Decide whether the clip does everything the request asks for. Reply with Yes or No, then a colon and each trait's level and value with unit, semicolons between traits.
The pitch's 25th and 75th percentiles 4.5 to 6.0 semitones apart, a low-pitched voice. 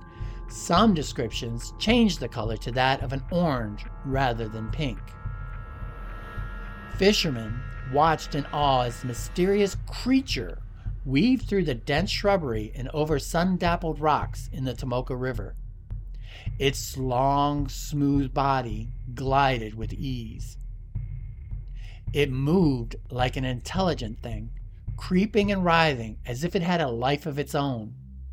Yes: average, 5.0 semitones; low, 130 Hz